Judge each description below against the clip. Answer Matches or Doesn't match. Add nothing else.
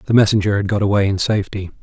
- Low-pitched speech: Matches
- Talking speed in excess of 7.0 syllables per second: Matches